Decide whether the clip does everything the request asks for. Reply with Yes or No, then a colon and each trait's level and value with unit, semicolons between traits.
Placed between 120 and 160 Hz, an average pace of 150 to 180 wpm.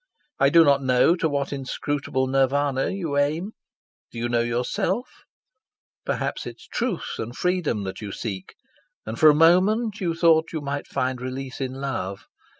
Yes: medium, 140 Hz; average, 170 wpm